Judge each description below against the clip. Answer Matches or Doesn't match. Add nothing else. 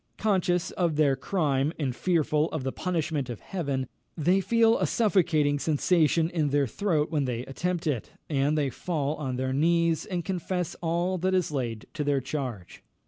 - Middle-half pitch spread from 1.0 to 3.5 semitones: Doesn't match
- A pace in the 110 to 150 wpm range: Doesn't match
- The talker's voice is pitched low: Doesn't match